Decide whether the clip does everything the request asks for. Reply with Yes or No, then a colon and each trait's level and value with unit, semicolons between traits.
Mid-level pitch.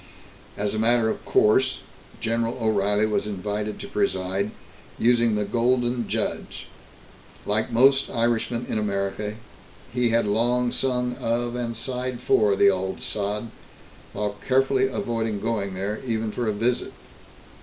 No: low, 115 Hz